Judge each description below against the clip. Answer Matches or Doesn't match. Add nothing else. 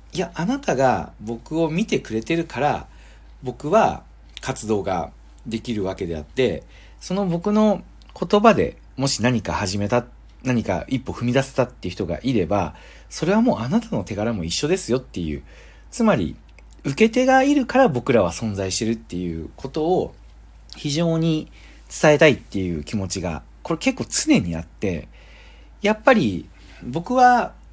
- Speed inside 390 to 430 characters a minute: Doesn't match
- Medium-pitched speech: Doesn't match